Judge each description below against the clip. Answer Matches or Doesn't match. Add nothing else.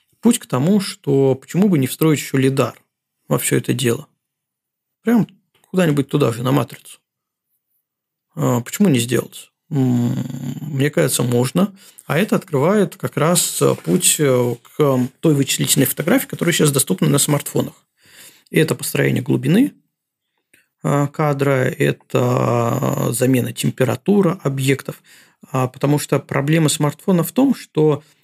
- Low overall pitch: Doesn't match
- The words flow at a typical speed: Matches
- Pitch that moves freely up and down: Doesn't match